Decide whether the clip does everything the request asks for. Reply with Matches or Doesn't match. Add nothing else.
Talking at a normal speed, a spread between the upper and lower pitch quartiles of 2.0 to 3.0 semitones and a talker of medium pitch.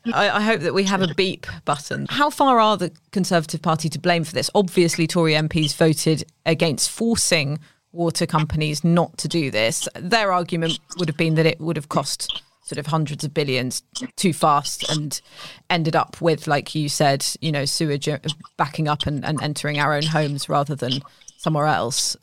Matches